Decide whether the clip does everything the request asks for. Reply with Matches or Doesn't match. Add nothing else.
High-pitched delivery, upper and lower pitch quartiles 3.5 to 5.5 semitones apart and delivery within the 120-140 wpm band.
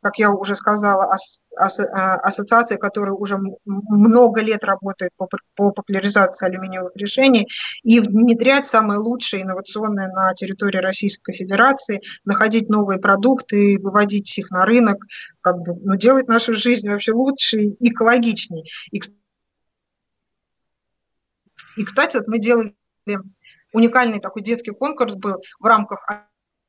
Doesn't match